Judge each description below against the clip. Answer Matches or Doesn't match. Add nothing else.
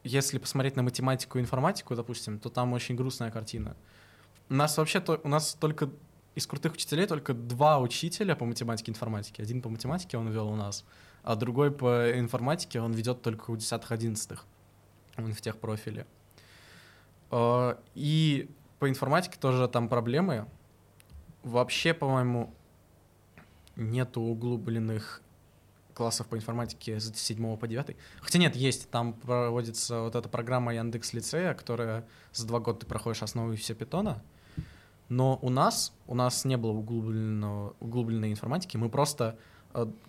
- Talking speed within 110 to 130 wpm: Doesn't match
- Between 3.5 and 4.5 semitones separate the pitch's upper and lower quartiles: Doesn't match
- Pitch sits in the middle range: Doesn't match